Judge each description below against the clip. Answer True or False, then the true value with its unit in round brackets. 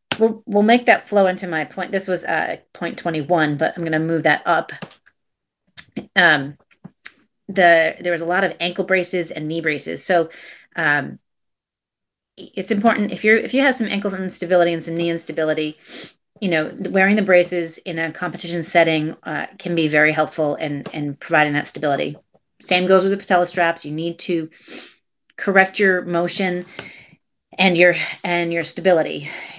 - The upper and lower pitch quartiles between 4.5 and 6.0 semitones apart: False (2.8 semitones)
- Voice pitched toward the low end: False (175 Hz)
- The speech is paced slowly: False (170 wpm)